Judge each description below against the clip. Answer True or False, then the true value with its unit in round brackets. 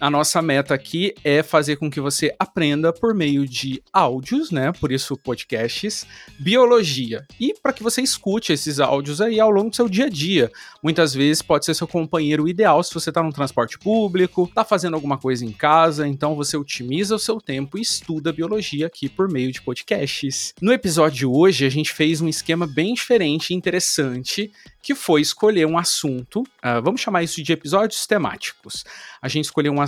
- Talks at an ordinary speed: False (195 wpm)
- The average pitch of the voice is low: False (160 Hz)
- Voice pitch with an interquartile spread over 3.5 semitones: True (5.4 semitones)